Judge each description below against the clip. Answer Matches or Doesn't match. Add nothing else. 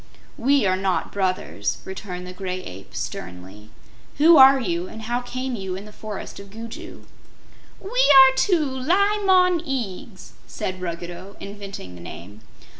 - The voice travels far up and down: Matches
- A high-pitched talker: Matches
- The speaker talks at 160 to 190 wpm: Doesn't match